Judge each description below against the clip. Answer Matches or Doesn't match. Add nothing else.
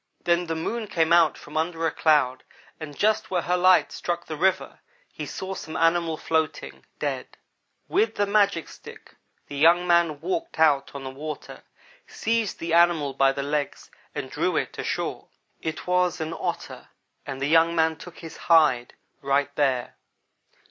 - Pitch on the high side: Doesn't match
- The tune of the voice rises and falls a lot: Doesn't match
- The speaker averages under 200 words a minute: Matches